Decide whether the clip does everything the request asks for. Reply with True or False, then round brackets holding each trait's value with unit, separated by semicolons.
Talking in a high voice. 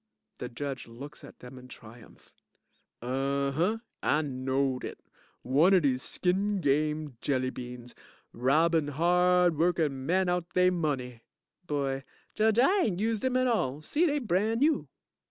False (150 Hz)